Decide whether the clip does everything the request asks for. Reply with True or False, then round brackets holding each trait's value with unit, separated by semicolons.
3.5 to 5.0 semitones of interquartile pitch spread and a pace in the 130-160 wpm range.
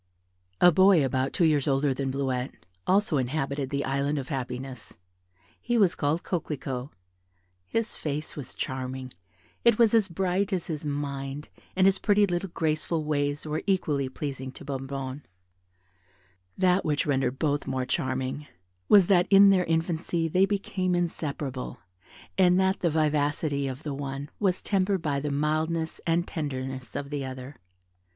True (4.6 semitones; 150 wpm)